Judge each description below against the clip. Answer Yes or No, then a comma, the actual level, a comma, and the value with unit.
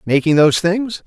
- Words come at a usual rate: Yes, average, 170 wpm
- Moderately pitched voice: Yes, medium, 175 Hz